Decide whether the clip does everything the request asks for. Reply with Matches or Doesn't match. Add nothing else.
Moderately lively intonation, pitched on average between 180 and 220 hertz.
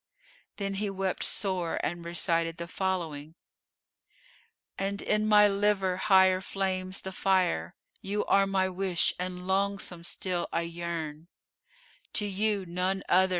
Doesn't match